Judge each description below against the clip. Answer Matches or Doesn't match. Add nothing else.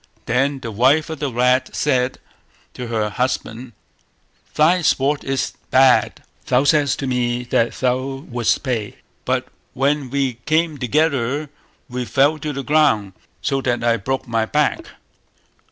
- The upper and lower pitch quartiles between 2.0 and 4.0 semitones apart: Matches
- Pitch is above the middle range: Doesn't match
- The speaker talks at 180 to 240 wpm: Doesn't match